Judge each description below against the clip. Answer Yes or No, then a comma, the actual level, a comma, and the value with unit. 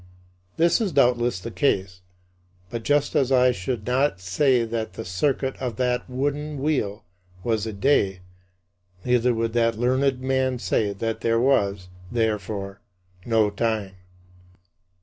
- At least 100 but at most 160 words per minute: Yes, average, 140 wpm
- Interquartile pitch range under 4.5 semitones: Yes, average, 4.1 semitones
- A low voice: Yes, low, 120 Hz